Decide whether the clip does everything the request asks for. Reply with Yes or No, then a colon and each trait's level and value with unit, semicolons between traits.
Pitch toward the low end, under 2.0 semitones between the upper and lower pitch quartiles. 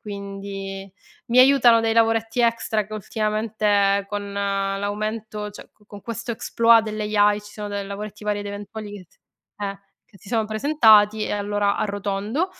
No: high, 210 Hz; narrow, 1.6 semitones